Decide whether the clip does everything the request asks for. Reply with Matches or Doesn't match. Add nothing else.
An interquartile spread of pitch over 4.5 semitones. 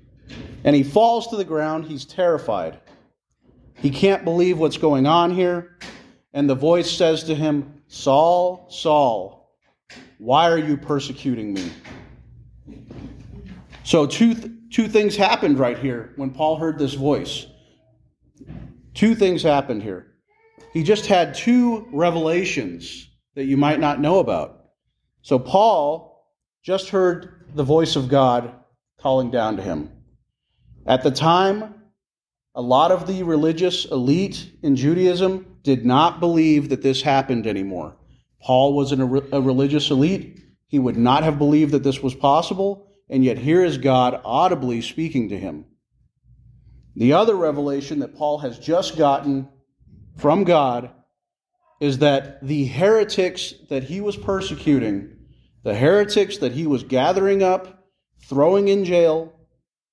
Matches